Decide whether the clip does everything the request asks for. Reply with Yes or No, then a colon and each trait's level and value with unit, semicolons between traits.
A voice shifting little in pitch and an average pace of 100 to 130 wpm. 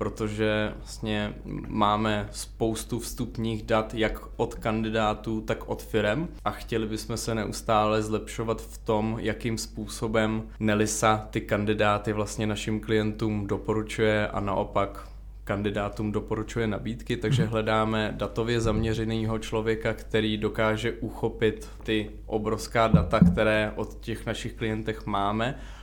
Yes: narrow, 0.9 semitones; average, 120 wpm